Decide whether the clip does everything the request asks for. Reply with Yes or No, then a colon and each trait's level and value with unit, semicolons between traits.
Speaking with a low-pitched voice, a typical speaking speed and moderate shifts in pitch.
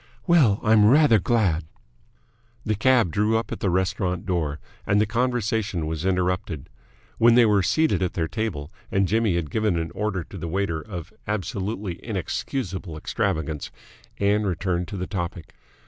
Yes: low, 100 Hz; average, 160 wpm; average, 4.0 semitones